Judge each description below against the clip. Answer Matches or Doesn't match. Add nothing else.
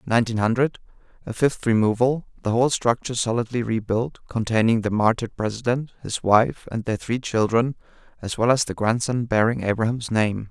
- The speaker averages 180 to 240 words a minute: Doesn't match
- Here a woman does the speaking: Doesn't match